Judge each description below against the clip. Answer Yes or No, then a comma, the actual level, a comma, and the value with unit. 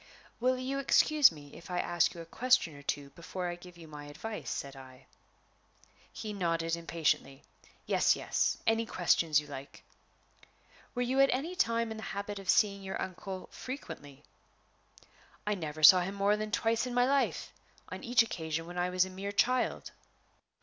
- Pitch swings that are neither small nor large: No, wide, 5.8 semitones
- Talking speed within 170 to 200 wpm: Yes, average, 175 wpm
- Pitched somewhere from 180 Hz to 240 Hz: Yes, medium, 185 Hz